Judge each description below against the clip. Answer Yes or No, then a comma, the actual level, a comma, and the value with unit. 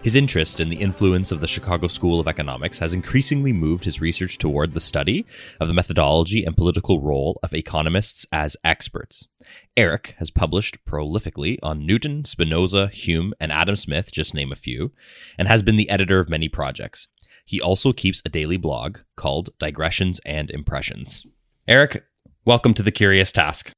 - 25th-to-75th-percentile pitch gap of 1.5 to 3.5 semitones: No, average, 4.2 semitones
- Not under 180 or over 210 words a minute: No, average, 170 wpm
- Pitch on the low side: Yes, very low, 90 Hz